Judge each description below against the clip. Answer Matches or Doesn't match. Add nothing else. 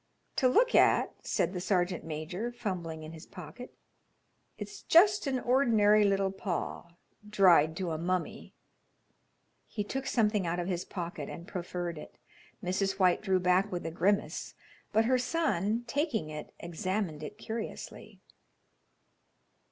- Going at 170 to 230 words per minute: Doesn't match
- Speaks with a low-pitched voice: Doesn't match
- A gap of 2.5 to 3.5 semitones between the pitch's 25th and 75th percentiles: Doesn't match